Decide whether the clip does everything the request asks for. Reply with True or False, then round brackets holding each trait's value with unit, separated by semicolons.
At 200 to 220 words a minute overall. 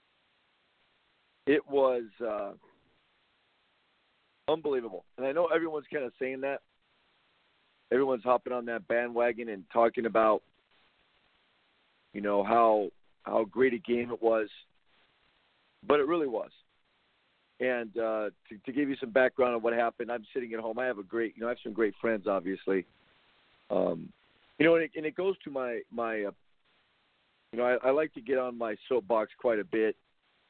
False (165 wpm)